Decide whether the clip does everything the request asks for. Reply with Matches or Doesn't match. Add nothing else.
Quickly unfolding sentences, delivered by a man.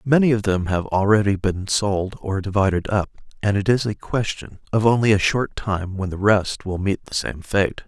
Matches